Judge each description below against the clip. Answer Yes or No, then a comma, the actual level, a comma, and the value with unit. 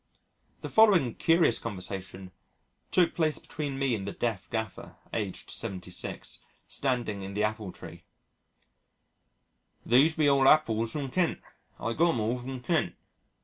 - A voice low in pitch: Yes, low, 120 Hz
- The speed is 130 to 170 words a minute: Yes, average, 140 wpm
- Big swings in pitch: Yes, wide, 5.7 semitones